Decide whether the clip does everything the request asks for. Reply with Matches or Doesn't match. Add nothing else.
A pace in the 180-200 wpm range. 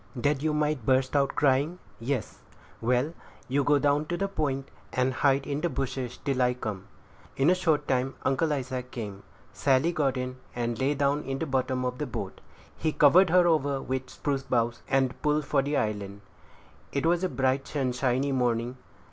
Matches